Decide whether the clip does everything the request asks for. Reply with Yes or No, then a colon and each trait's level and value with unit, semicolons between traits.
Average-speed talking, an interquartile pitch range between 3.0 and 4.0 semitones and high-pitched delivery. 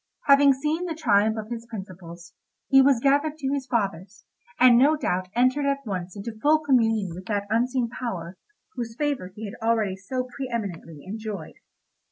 No: average, 175 wpm; wide, 5.5 semitones; high, 230 Hz